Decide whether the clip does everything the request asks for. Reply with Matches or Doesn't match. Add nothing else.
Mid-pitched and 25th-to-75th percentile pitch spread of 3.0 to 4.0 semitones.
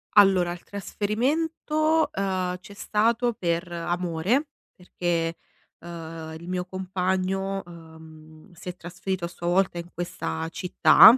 Doesn't match